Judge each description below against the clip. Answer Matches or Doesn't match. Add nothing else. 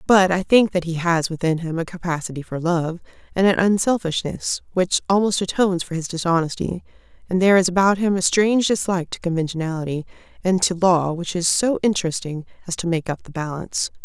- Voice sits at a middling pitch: Matches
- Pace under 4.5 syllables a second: Doesn't match